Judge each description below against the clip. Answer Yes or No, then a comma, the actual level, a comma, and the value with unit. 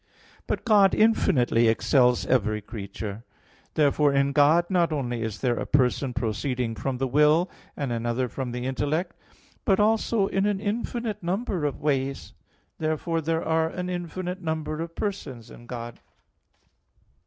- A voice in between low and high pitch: Yes, medium, 145 Hz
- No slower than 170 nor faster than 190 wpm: No, average, 145 wpm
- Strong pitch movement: Yes, wide, 6.2 semitones